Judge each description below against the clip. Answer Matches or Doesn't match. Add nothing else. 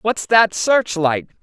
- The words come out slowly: Matches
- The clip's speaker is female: Matches